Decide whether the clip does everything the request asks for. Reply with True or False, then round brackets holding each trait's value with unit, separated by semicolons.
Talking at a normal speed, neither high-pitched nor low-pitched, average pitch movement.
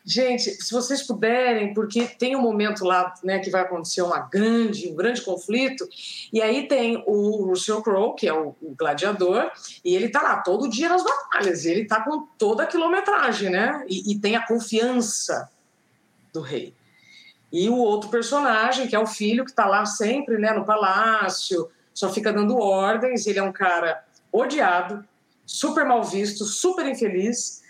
False (175 wpm; 220 Hz; 4.0 semitones)